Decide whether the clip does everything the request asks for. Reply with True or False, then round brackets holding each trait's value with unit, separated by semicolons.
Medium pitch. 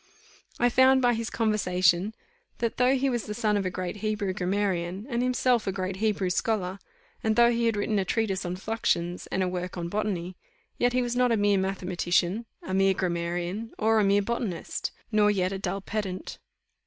False (205 Hz)